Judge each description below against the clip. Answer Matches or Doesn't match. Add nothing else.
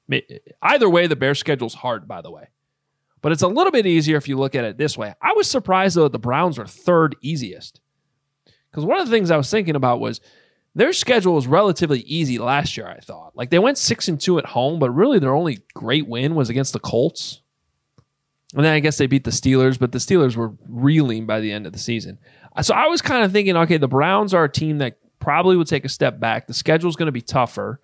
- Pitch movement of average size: Matches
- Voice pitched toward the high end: Doesn't match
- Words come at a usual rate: Doesn't match